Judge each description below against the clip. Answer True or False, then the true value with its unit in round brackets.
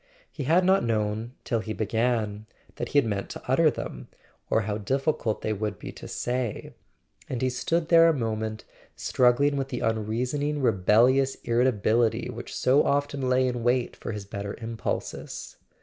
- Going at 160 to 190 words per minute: True (170 wpm)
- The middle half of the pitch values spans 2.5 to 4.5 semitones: True (3.6 semitones)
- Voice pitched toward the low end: True (120 Hz)